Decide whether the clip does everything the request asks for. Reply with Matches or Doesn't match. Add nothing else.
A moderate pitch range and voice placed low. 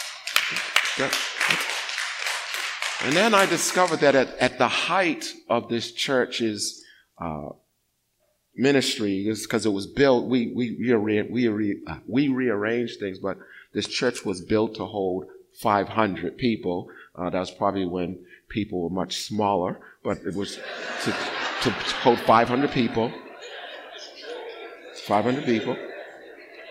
Matches